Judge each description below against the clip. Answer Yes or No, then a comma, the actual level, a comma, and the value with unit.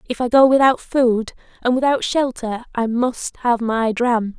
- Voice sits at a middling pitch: No, high, 240 Hz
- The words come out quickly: No, average, 180 wpm